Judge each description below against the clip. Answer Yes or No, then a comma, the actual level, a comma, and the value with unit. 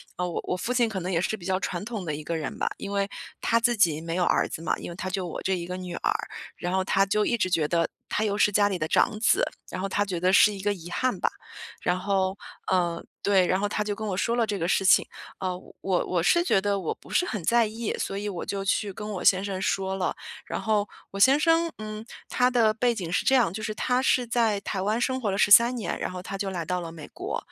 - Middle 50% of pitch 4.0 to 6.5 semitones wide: No, average, 3.1 semitones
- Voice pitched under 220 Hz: Yes, high, 200 Hz